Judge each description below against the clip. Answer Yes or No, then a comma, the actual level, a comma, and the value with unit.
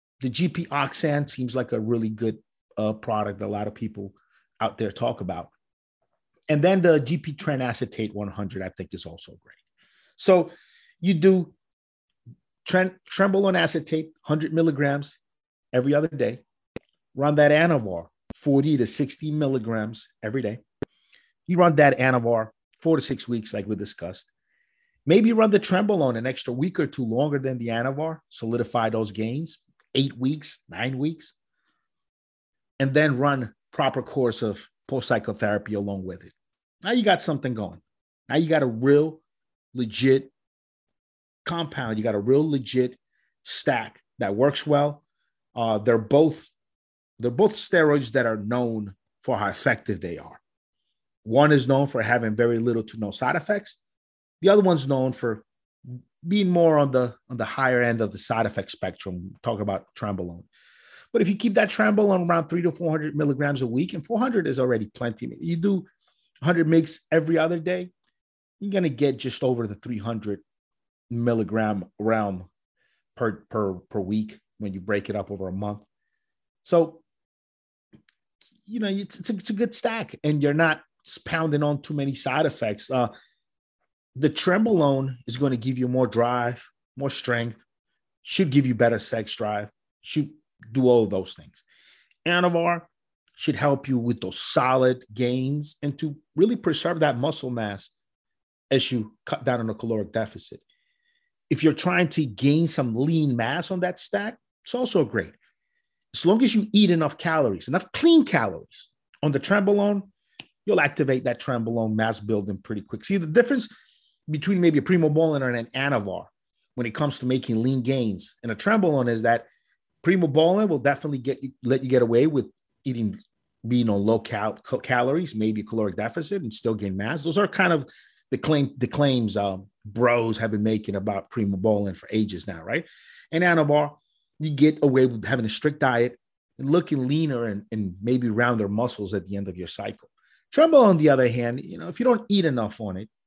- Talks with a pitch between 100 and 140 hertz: Yes, low, 135 Hz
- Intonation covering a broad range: Yes, wide, 6.4 semitones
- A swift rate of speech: No, average, 175 wpm